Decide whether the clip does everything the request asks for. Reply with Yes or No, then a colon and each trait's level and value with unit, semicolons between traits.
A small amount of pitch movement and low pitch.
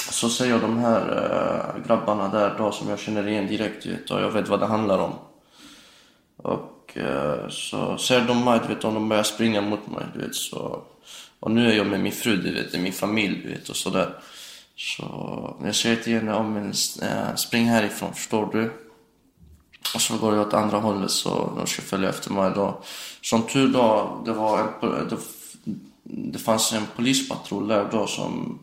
Yes: narrow, 1.8 semitones; low, 110 Hz